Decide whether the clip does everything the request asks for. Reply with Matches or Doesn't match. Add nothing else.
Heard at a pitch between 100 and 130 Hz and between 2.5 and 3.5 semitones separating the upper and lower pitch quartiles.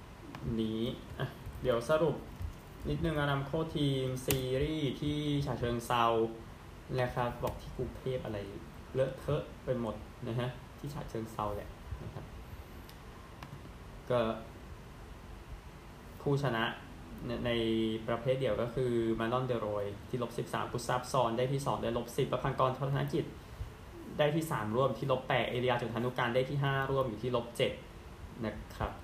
Matches